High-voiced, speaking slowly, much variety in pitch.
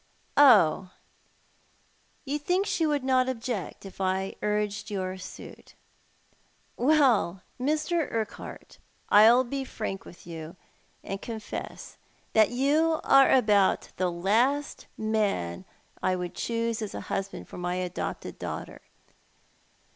Yes: high, 220 Hz; slow, 120 wpm; wide, 5.9 semitones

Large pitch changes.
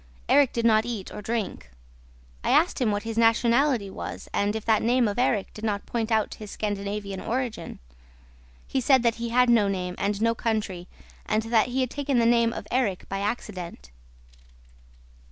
No: average, 2.7 semitones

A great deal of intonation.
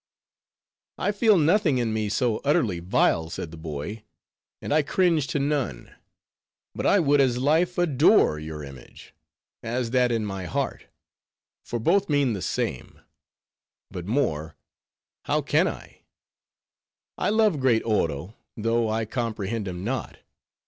Yes: wide, 7.1 semitones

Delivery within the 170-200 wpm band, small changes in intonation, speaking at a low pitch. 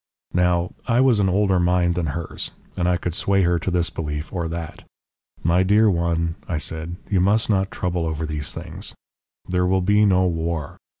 Yes: average, 190 wpm; narrow, 2.3 semitones; very low, 90 Hz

